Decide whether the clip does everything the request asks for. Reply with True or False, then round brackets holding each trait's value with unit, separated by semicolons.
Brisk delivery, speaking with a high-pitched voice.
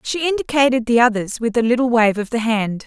True (230 wpm; 240 Hz)